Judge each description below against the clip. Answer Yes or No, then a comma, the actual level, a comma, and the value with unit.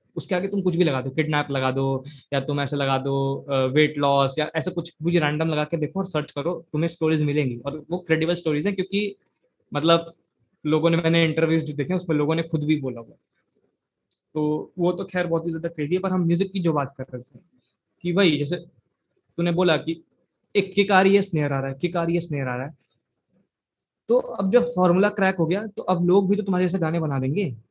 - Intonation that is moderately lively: Yes, average, 3.8 semitones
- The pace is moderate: No, fast, 215 wpm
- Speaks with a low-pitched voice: No, medium, 165 Hz